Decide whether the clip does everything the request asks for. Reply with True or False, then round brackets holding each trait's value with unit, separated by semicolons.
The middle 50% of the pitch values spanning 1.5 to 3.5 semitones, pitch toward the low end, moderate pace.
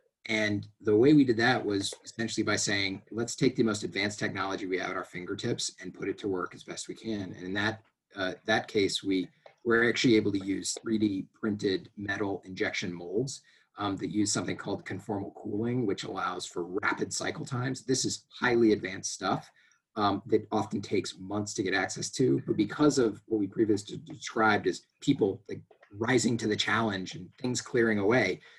True (2.7 semitones; 110 Hz; 195 wpm)